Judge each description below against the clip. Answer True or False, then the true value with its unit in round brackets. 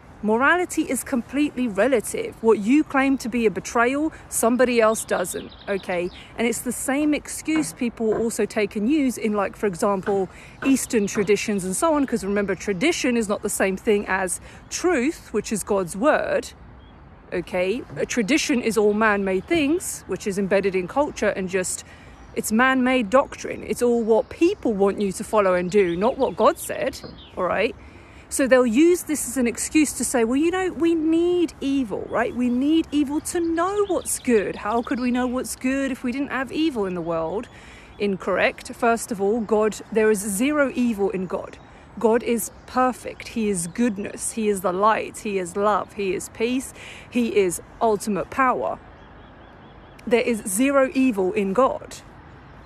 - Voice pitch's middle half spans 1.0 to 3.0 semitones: False (4.7 semitones)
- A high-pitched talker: True (235 Hz)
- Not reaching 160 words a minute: False (180 wpm)